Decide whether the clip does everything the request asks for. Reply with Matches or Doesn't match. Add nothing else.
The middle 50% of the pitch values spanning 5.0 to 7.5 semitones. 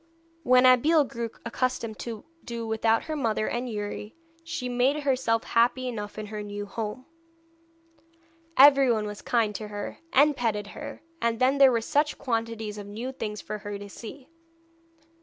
Doesn't match